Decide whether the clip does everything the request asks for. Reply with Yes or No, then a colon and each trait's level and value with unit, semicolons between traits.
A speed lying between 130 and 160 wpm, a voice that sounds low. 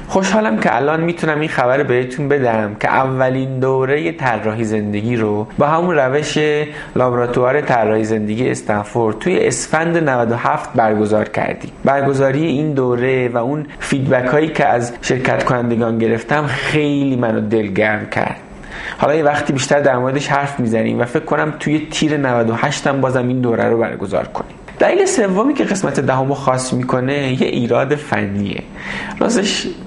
Yes: average, 150 wpm; low, 130 Hz